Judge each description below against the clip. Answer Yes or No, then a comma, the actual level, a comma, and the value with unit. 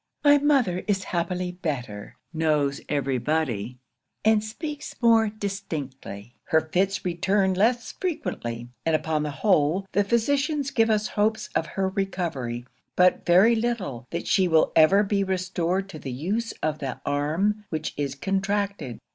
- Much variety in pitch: Yes, wide, 5.8 semitones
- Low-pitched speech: No, medium, 185 Hz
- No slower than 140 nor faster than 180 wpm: Yes, average, 145 wpm